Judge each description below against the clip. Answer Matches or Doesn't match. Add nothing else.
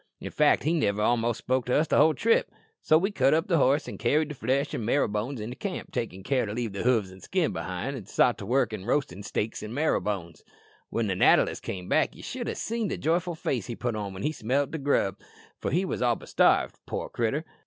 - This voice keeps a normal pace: Doesn't match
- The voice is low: Matches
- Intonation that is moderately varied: Doesn't match